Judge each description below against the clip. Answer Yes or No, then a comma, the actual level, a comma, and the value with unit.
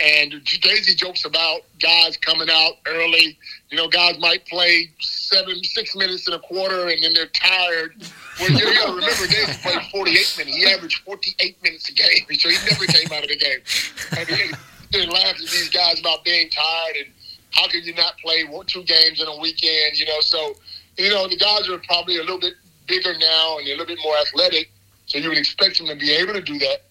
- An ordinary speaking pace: No, fast, 215 wpm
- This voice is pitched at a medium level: Yes, medium, 170 Hz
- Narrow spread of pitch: Yes, narrow, 2.2 semitones